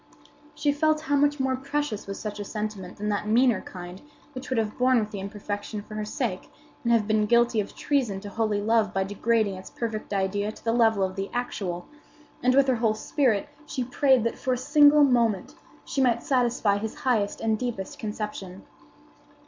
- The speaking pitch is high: Yes, high, 220 Hz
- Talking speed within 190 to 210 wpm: Yes, average, 195 wpm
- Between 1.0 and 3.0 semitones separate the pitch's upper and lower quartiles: No, average, 3.8 semitones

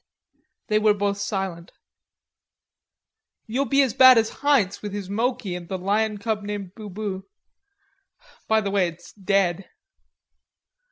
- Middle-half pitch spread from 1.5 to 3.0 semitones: Yes, narrow, 2.4 semitones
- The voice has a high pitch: Yes, high, 205 Hz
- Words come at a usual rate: No, slow, 130 wpm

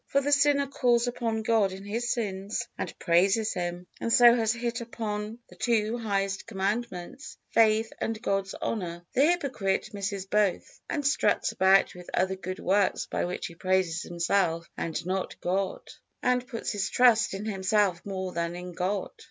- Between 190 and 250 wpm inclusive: No, average, 170 wpm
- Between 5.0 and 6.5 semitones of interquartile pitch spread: No, average, 3.8 semitones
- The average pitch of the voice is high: Yes, high, 200 Hz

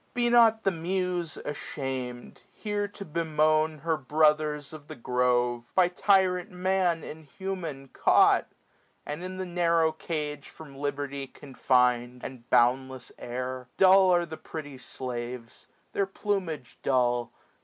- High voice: No, medium, 155 Hz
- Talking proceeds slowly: Yes, slow, 130 wpm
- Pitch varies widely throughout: Yes, wide, 5.8 semitones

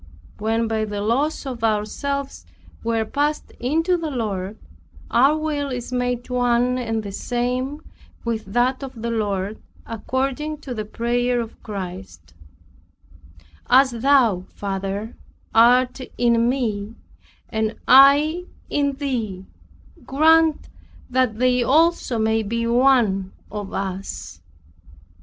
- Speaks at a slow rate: Yes, slow, 120 wpm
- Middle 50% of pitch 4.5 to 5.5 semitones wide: No, average, 3.7 semitones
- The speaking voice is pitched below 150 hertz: No, high, 240 Hz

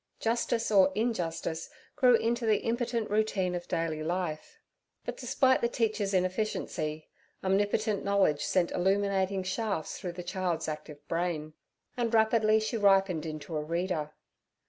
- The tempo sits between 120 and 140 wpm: Yes, slow, 135 wpm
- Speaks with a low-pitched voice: No, high, 190 Hz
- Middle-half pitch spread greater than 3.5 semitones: Yes, average, 4.4 semitones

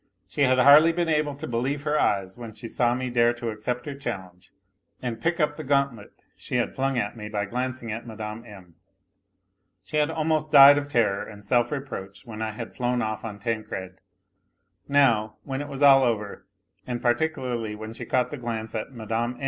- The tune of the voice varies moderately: Yes, average, 4.2 semitones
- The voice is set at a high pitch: No, low, 120 Hz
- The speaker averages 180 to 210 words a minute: Yes, average, 200 wpm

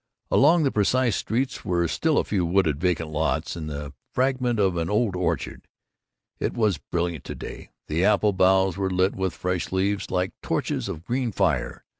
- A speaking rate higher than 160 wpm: Yes, average, 180 wpm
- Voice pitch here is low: Yes, very low, 95 Hz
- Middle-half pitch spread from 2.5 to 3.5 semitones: No, average, 3.9 semitones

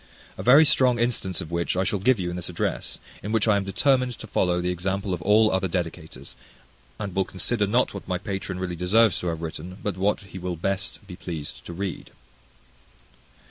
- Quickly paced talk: Yes, fast, 210 wpm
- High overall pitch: No, very low, 95 Hz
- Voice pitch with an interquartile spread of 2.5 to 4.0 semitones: Yes, average, 2.9 semitones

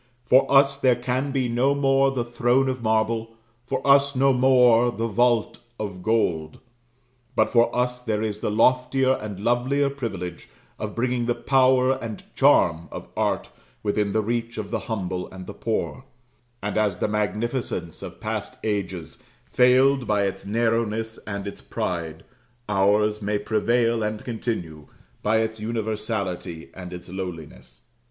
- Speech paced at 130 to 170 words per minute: Yes, average, 150 wpm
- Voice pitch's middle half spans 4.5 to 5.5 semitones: No, average, 3.5 semitones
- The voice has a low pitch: Yes, low, 110 Hz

